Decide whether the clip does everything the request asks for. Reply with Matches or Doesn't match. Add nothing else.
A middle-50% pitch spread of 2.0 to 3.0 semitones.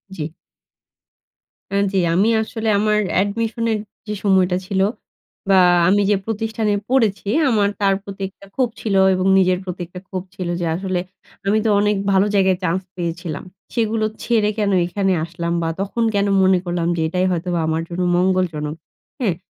Matches